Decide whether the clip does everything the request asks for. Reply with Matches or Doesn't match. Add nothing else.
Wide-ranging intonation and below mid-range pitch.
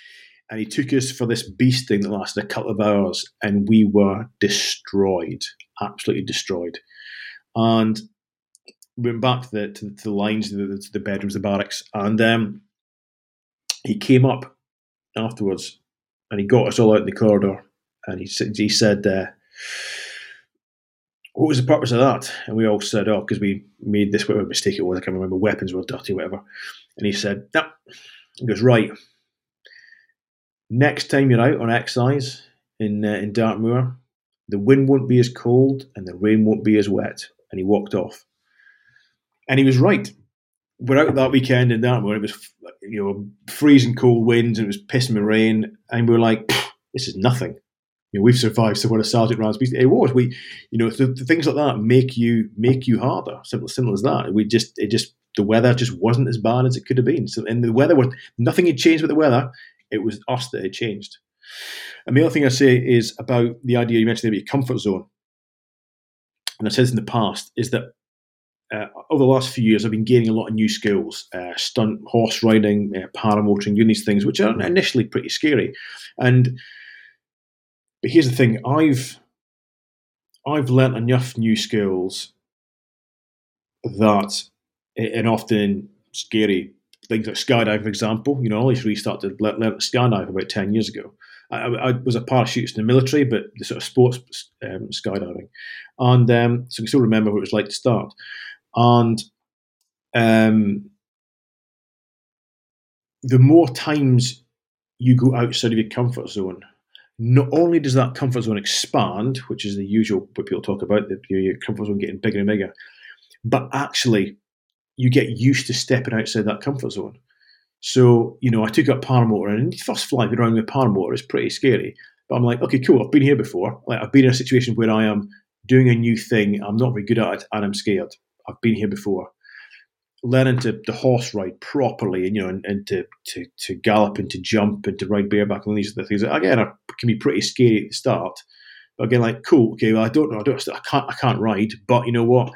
Doesn't match